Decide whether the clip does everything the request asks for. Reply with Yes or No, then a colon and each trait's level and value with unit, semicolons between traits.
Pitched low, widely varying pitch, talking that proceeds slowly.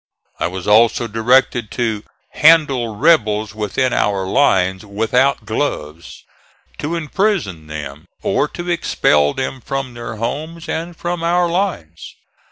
Yes: low, 120 Hz; wide, 7.6 semitones; slow, 125 wpm